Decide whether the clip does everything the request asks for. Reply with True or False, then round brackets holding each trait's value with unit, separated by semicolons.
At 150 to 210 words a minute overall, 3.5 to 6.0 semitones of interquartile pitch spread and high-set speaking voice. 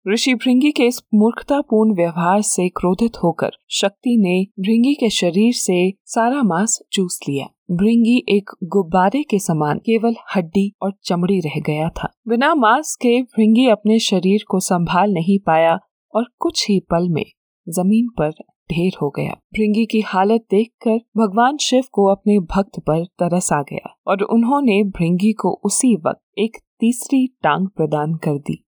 True (160 wpm; 4.1 semitones; 205 Hz)